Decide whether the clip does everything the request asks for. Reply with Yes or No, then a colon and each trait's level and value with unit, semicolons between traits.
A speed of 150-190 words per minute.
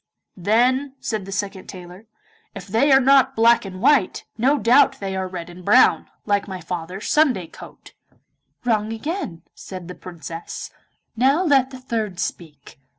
Yes: average, 155 wpm